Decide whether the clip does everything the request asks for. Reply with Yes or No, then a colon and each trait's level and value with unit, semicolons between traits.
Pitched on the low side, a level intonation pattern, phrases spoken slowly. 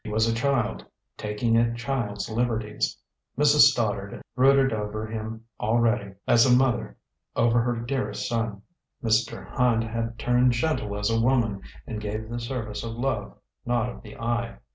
No: low, 115 Hz; narrow, 1.8 semitones; average, 160 wpm